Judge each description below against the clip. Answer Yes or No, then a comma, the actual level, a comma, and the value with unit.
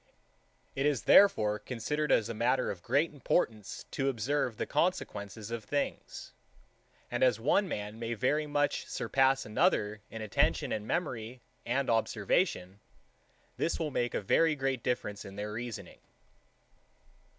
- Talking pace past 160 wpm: No, average, 140 wpm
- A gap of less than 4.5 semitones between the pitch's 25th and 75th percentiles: No, average, 5.0 semitones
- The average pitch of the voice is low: Yes, low, 120 Hz